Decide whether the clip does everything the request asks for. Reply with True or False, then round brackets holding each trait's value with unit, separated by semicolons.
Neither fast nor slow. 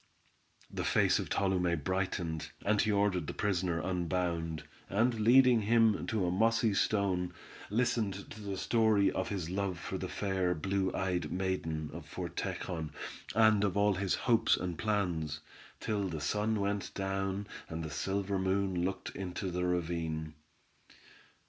True (150 wpm)